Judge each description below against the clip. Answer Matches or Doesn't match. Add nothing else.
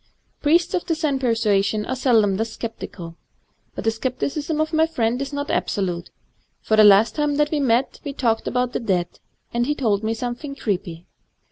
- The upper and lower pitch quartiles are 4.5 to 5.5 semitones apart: Matches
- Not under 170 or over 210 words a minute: Matches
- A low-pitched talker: Doesn't match